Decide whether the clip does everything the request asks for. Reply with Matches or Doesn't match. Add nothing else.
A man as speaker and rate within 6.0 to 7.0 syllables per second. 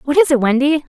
Doesn't match